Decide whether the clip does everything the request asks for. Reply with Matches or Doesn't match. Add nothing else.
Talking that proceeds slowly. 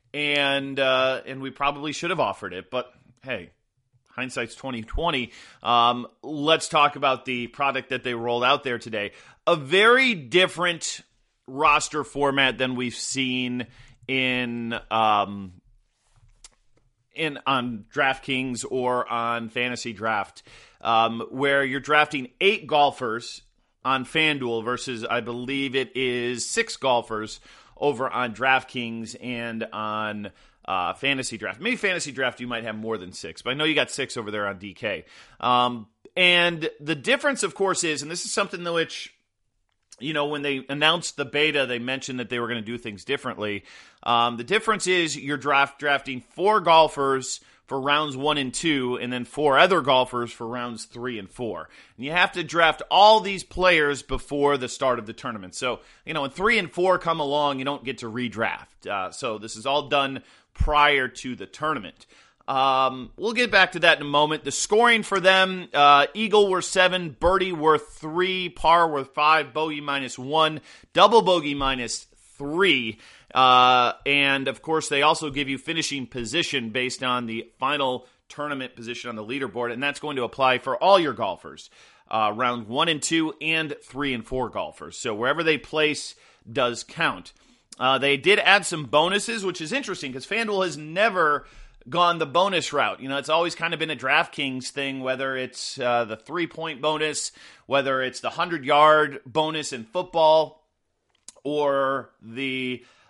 Doesn't match